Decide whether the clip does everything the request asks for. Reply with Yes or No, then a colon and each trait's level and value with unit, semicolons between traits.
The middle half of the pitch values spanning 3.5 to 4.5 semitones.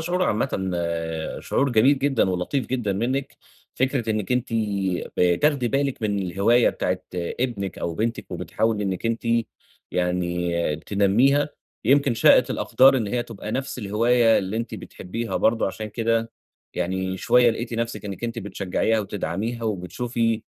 Yes: average, 4.1 semitones